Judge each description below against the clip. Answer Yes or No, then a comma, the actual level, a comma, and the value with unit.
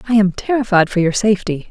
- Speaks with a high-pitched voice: Yes, high, 200 Hz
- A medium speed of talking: No, fast, 210 wpm